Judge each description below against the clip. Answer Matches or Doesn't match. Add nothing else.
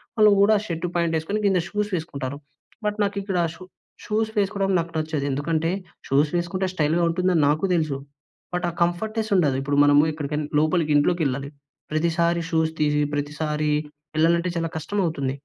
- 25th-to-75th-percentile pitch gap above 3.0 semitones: Matches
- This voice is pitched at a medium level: Matches